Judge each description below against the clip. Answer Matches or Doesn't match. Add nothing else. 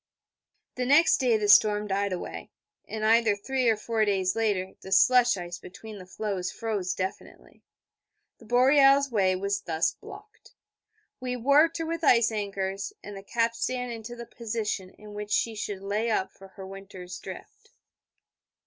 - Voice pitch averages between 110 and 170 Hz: Doesn't match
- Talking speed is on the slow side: Doesn't match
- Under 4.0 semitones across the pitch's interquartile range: Matches